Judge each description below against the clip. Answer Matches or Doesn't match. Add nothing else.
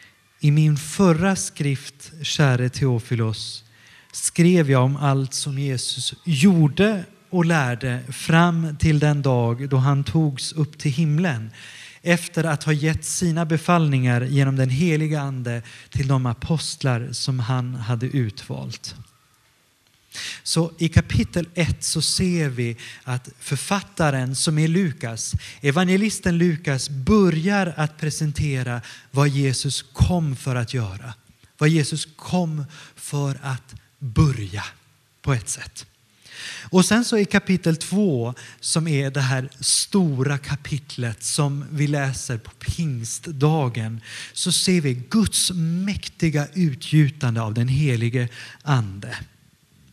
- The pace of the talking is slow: Matches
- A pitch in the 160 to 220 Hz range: Doesn't match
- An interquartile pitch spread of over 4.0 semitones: Matches